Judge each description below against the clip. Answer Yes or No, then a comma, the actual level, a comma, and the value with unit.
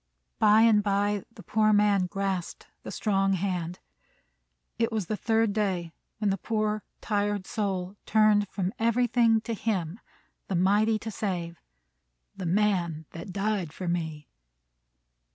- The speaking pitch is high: Yes, high, 205 Hz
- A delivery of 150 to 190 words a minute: No, slow, 135 wpm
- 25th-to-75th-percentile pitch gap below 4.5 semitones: Yes, average, 2.8 semitones